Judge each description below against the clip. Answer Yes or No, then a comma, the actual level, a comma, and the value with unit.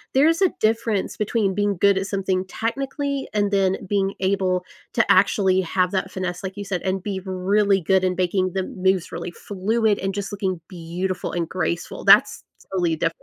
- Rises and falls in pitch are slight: Yes, narrow, 1.8 semitones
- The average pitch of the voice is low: No, high, 190 Hz